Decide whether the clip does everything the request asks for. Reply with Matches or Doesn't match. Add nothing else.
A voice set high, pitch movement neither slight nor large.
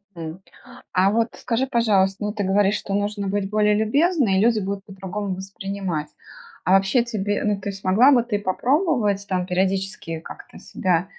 Doesn't match